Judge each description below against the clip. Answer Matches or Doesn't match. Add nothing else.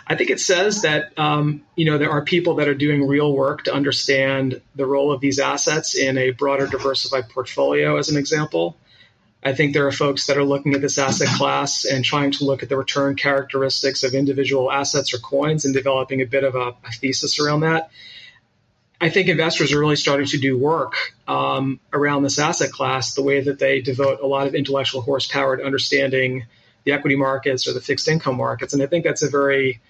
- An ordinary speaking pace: Doesn't match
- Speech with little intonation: Matches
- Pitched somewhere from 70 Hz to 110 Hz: Doesn't match